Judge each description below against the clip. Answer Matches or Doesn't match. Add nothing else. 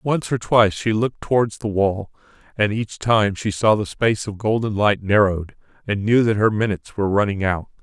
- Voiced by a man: Matches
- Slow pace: Doesn't match